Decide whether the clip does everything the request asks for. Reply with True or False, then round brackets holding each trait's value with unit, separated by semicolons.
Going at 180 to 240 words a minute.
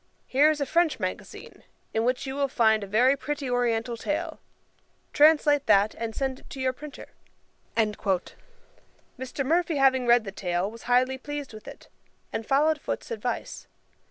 False (160 wpm)